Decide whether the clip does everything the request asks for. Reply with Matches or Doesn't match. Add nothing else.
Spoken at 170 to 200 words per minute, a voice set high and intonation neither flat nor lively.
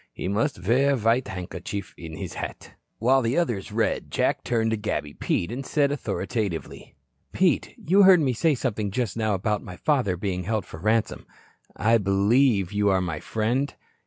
Doesn't match